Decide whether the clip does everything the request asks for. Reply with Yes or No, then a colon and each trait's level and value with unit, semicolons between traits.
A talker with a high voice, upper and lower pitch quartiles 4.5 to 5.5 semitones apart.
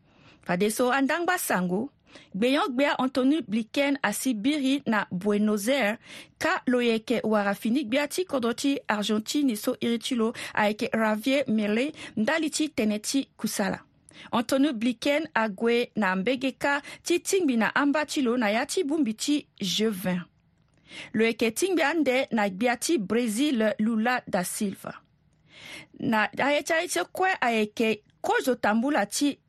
Yes: high, 245 Hz; average, 5.0 semitones